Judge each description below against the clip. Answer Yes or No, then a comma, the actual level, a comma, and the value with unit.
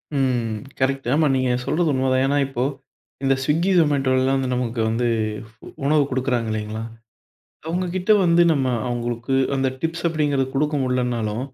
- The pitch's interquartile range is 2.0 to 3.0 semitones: No, average, 3.5 semitones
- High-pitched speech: No, low, 135 Hz